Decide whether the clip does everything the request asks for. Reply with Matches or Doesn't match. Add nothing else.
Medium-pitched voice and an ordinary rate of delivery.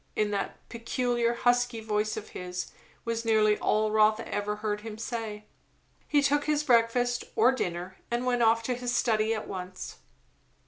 Doesn't match